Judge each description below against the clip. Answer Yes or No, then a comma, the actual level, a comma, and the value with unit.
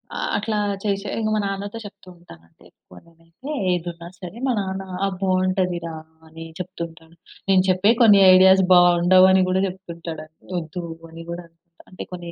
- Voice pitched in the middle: Yes, medium, 180 Hz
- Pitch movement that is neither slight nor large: No, narrow, 2.2 semitones